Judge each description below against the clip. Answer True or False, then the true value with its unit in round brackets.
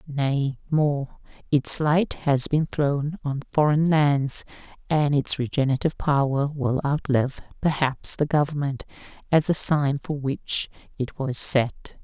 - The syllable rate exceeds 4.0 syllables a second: False (3.9 syllables/s)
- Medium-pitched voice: True (145 Hz)